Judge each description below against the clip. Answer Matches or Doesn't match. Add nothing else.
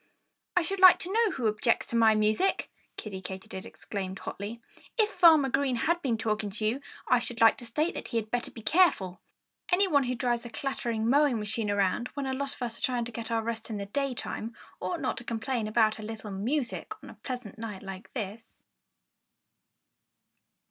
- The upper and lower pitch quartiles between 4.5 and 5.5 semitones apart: Doesn't match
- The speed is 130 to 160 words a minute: Doesn't match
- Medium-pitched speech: Doesn't match